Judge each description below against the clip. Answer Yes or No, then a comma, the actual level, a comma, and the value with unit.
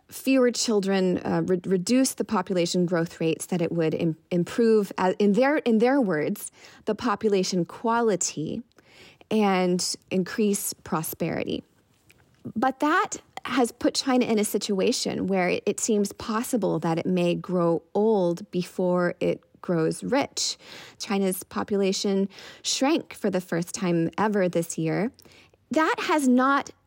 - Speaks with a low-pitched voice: No, high, 200 Hz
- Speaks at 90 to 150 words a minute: Yes, slow, 135 wpm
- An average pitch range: Yes, average, 4.7 semitones